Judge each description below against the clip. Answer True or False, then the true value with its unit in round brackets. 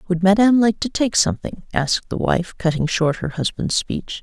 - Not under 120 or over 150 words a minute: False (200 wpm)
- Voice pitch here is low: False (185 Hz)